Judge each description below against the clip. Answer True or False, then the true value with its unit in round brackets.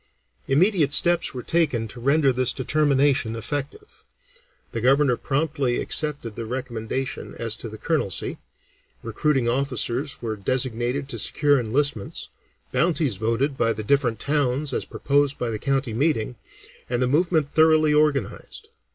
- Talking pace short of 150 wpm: True (135 wpm)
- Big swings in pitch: False (3.9 semitones)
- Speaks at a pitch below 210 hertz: True (135 Hz)